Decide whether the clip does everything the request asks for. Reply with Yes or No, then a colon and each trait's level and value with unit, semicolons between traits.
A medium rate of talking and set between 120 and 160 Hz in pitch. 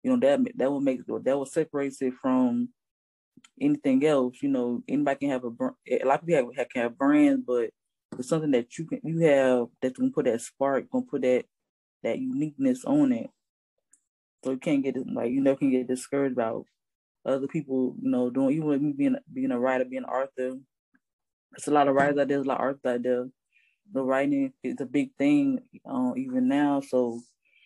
No: fast, 215 wpm; medium, 140 Hz